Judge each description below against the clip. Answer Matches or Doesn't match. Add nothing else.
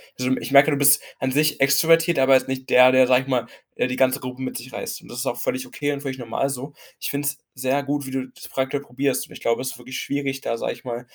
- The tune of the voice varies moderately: Doesn't match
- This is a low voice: Matches